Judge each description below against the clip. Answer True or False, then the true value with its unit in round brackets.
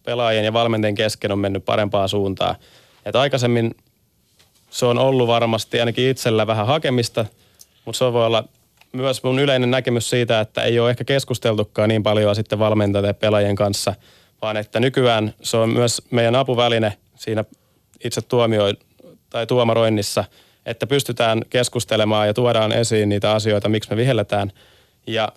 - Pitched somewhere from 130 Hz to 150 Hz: False (115 Hz)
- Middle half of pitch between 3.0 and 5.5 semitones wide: False (2.4 semitones)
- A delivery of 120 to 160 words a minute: True (150 wpm)